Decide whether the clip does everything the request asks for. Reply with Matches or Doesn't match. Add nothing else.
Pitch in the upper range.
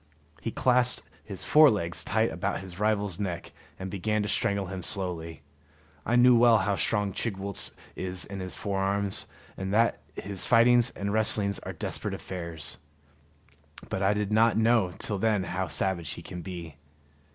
Doesn't match